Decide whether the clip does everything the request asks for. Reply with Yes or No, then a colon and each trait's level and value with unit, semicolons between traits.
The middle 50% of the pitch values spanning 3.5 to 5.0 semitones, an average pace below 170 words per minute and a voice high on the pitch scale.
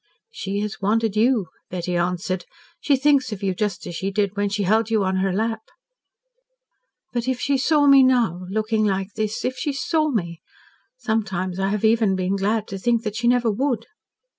No: average, 3.9 semitones; average, 190 wpm; high, 215 Hz